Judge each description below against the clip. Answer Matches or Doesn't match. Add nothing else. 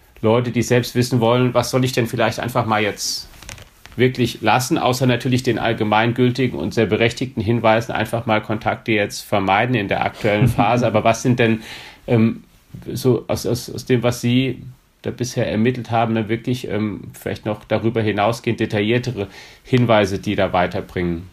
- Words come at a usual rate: Matches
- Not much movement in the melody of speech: Matches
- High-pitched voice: Doesn't match